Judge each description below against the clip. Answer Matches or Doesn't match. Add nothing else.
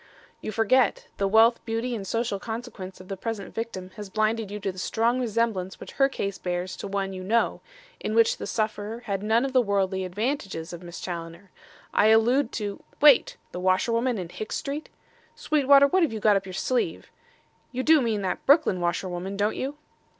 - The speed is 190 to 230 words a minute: Matches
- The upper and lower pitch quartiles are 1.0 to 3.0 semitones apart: Doesn't match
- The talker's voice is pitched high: Matches